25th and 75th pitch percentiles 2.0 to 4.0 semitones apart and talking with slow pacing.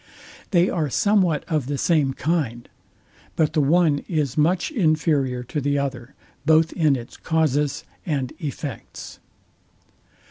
Yes: average, 2.9 semitones; slow, 130 wpm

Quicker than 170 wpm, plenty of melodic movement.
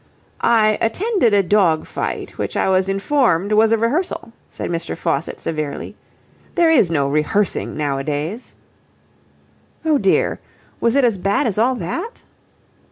No: average, 140 wpm; wide, 6.7 semitones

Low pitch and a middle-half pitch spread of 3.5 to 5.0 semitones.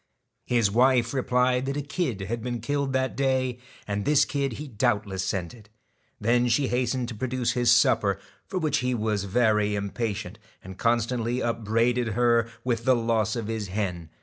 No: low, 120 Hz; average, 3.1 semitones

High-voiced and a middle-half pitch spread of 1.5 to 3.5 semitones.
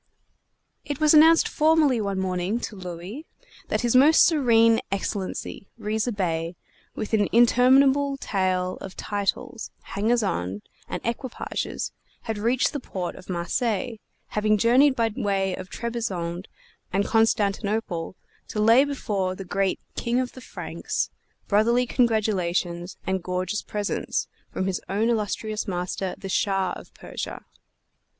No: high, 210 Hz; average, 4.2 semitones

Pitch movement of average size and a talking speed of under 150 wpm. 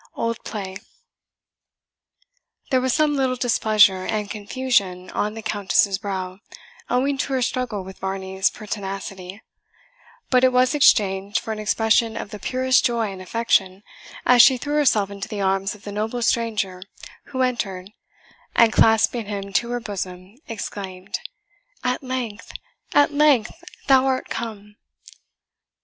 Yes: average, 4.3 semitones; average, 140 wpm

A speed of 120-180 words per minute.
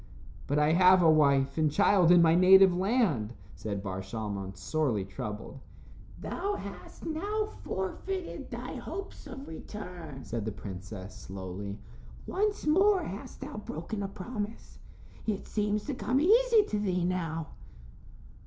Yes: average, 140 wpm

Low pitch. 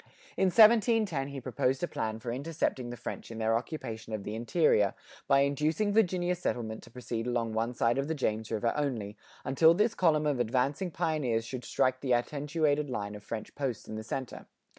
Yes: low, 130 Hz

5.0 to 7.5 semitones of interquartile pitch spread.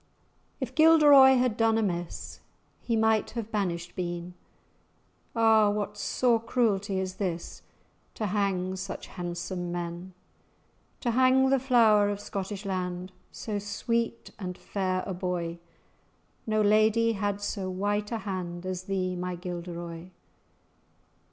No: average, 3.6 semitones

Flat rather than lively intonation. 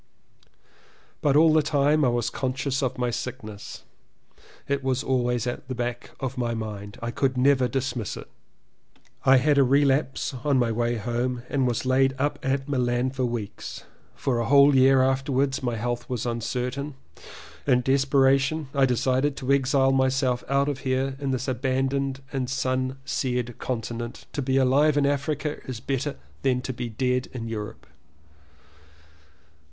Yes: narrow, 1.9 semitones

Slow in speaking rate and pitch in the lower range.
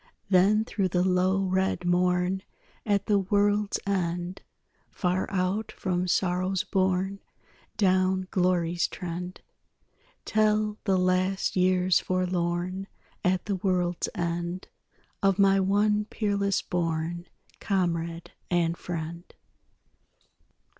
No: slow, 100 wpm; medium, 185 Hz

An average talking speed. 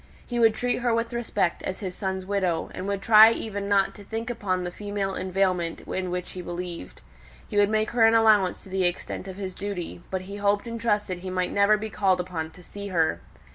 No: fast, 225 wpm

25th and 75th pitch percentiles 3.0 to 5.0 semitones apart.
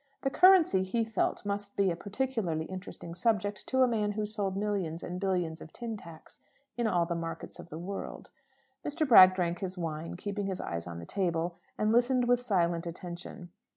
Yes: average, 4.3 semitones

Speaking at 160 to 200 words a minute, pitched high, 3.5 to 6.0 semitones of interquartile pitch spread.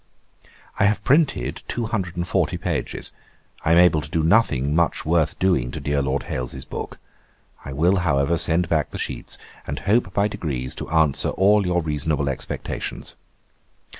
No: average, 165 wpm; very low, 80 Hz; average, 4.5 semitones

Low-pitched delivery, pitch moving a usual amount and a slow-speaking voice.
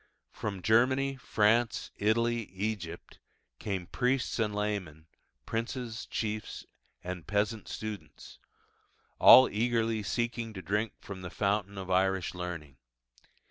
Yes: low, 105 Hz; average, 3.2 semitones; slow, 110 wpm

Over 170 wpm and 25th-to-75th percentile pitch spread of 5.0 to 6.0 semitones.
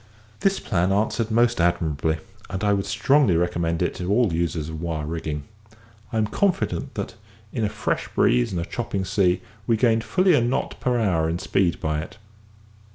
Yes: average, 185 wpm; wide, 5.5 semitones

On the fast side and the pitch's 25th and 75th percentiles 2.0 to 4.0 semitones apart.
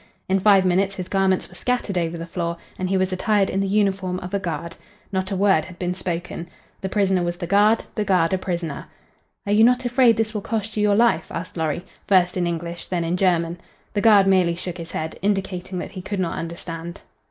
Yes: fast, 225 wpm; narrow, 2.6 semitones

